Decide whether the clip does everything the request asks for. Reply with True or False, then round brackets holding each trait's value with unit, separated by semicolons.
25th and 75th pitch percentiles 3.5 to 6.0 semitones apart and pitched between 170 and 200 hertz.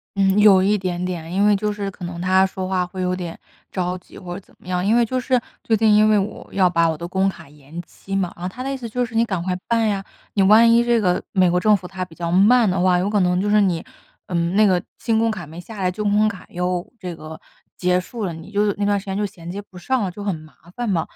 False (2.8 semitones; 190 Hz)